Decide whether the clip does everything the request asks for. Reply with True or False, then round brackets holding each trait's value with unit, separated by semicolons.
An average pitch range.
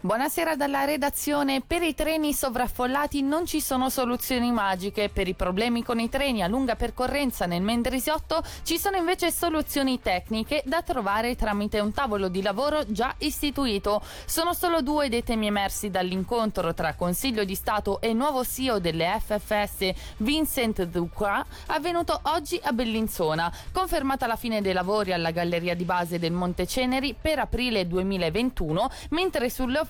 False (6.4 semitones)